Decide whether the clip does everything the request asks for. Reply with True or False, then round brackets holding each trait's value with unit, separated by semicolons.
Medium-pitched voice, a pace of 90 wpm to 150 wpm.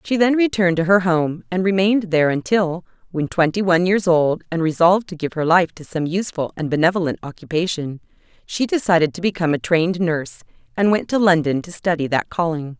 False (175 Hz; 195 wpm)